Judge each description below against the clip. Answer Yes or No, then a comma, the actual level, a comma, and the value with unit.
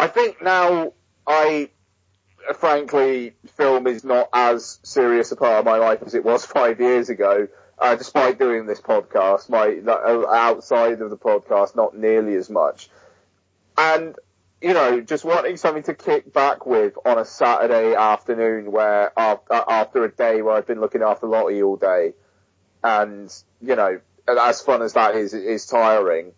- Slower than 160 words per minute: No, average, 165 wpm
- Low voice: Yes, low, 115 Hz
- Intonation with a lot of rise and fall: Yes, wide, 6.1 semitones